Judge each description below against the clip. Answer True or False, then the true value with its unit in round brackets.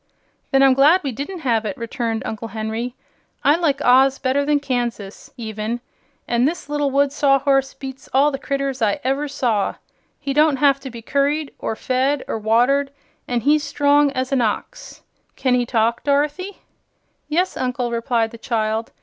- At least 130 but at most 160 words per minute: False (170 wpm)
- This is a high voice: True (270 Hz)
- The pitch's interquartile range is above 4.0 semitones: False (3.3 semitones)